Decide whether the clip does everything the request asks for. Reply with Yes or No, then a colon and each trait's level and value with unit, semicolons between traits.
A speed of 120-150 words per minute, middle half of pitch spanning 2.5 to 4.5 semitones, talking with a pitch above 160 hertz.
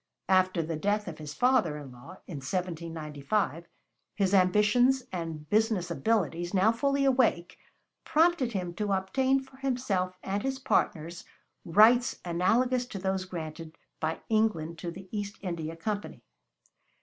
No: slow, 135 wpm; average, 5.2 semitones; high, 190 Hz